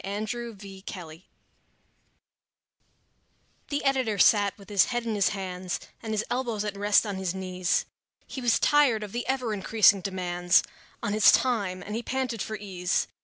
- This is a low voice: No, high, 205 Hz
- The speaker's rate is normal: Yes, average, 170 wpm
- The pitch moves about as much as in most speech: Yes, average, 3.6 semitones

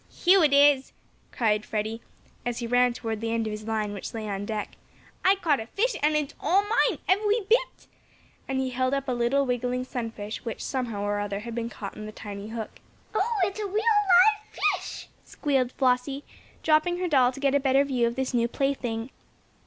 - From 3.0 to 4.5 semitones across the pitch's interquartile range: No, wide, 5.5 semitones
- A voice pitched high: Yes, very high, 255 Hz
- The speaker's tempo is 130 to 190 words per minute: No, fast, 205 wpm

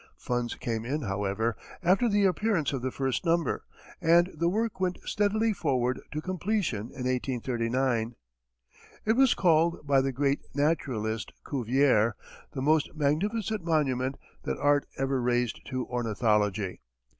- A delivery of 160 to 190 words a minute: No, slow, 135 wpm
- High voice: No, low, 135 Hz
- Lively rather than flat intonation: Yes, wide, 5.9 semitones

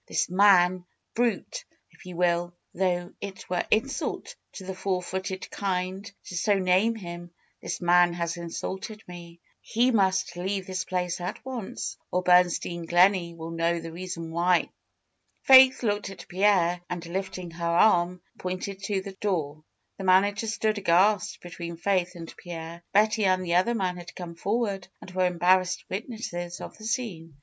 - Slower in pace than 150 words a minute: No, average, 165 wpm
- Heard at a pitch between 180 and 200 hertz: Yes, medium, 185 Hz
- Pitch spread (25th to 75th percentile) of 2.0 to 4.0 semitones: Yes, narrow, 2.4 semitones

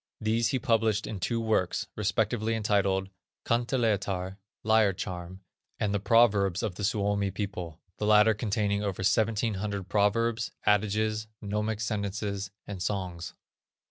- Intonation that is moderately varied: No, narrow, 2.0 semitones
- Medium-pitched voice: No, low, 105 Hz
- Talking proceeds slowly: Yes, slow, 125 wpm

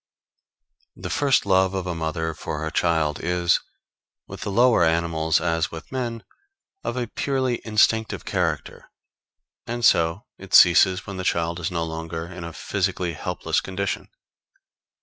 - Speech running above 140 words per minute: Yes, average, 150 wpm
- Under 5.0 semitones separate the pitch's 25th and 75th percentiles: Yes, average, 3.7 semitones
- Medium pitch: No, very low, 90 Hz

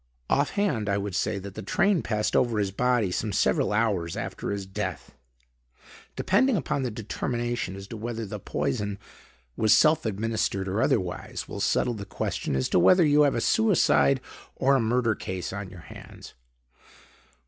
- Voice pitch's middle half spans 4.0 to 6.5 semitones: Yes, average, 4.4 semitones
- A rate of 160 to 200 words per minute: Yes, average, 170 wpm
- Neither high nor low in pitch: No, low, 110 Hz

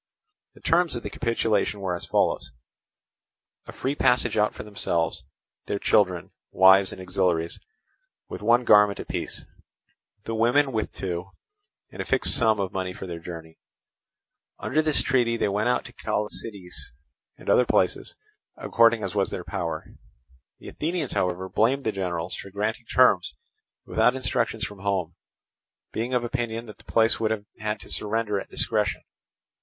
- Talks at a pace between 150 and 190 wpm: Yes, average, 160 wpm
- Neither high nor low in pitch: No, low, 105 Hz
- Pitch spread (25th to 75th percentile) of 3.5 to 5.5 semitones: Yes, average, 3.9 semitones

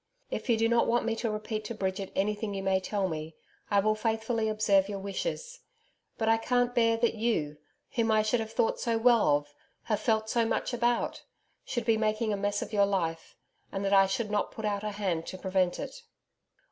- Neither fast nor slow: No, fast, 215 wpm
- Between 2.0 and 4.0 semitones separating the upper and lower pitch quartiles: Yes, narrow, 2.6 semitones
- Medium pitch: No, high, 215 Hz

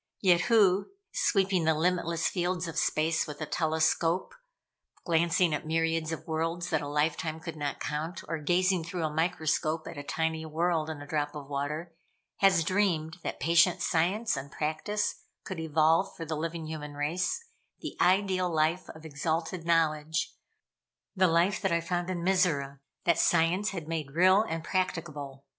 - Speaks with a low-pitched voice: No, medium, 165 Hz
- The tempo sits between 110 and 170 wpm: Yes, average, 165 wpm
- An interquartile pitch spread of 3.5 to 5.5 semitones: No, narrow, 2.4 semitones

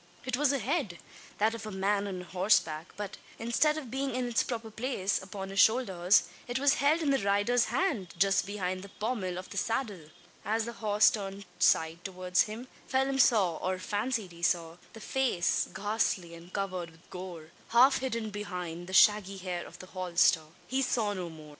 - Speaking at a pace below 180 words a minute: No, average, 190 wpm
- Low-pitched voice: No, high, 200 Hz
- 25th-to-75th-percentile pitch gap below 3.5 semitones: No, average, 4.5 semitones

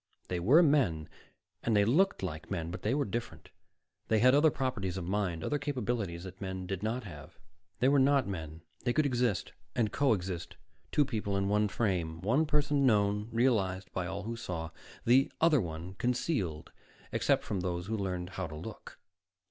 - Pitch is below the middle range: Yes, low, 105 Hz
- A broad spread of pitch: Yes, wide, 5.8 semitones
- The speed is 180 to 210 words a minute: Yes, average, 185 wpm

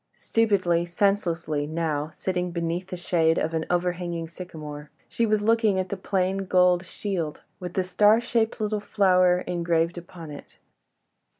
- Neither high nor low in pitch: Yes, medium, 180 Hz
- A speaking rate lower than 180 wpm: Yes, average, 145 wpm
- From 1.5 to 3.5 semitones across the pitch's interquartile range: Yes, average, 2.7 semitones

